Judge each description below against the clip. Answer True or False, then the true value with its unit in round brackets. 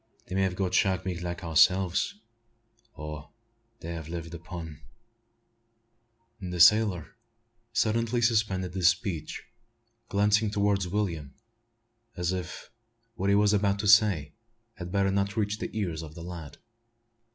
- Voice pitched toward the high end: False (95 Hz)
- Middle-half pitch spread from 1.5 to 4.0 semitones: True (3.3 semitones)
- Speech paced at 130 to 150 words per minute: True (140 wpm)